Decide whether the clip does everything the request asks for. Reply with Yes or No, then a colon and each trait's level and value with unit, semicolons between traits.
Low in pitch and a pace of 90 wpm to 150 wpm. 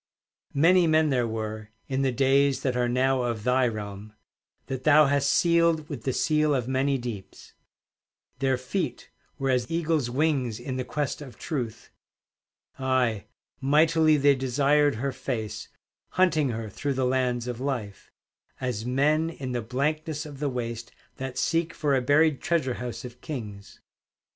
No: low, 130 Hz; average, 160 wpm